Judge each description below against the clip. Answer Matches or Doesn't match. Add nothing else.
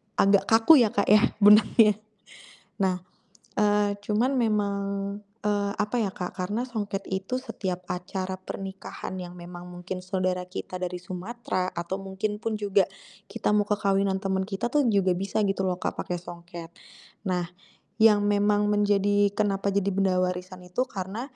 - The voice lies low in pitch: Doesn't match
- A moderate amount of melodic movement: Doesn't match